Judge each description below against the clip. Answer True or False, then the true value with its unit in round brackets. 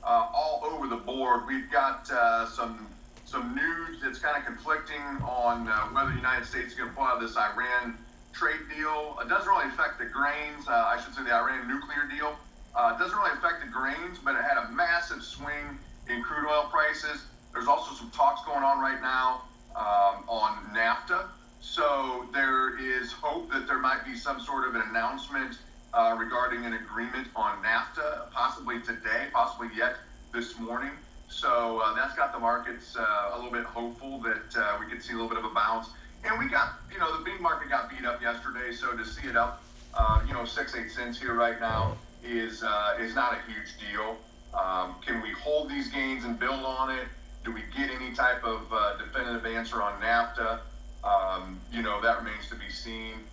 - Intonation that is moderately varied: True (4.2 semitones)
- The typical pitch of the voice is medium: False (125 Hz)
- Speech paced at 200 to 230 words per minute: True (205 wpm)